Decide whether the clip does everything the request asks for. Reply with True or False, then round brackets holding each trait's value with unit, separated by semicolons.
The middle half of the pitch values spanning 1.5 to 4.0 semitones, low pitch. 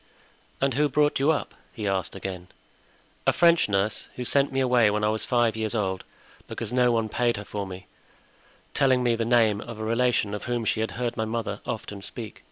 True (3.1 semitones; 115 Hz)